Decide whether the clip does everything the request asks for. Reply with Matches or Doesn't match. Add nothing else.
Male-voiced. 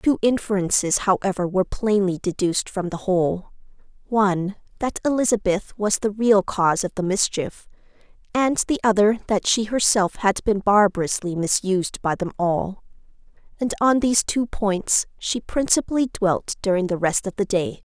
Doesn't match